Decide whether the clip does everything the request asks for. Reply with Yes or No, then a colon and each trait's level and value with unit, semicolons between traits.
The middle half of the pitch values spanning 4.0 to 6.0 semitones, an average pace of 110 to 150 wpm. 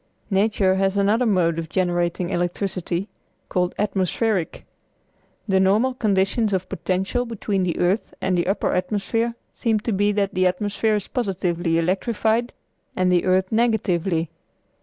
No: average, 3.0 semitones; average, 140 wpm